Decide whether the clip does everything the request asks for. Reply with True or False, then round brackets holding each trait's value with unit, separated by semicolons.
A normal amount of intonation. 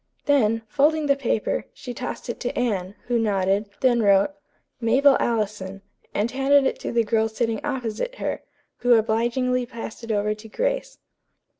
True (3.7 semitones)